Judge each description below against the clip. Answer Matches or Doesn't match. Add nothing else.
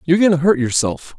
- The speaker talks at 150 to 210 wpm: Doesn't match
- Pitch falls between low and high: Matches